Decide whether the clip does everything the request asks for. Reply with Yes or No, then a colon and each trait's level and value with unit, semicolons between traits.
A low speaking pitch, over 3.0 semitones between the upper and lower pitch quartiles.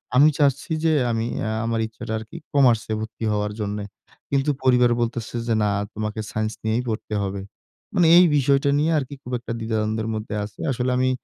Yes: low, 115 Hz; average, 3.5 semitones